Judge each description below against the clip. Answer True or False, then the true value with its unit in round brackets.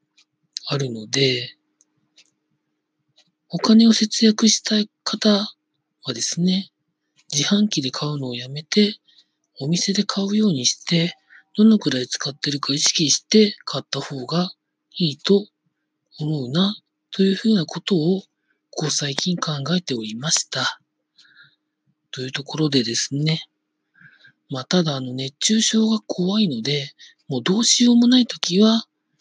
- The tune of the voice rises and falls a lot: True (6.4 semitones)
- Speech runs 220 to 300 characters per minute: True (245 characters per minute)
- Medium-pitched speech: True (165 Hz)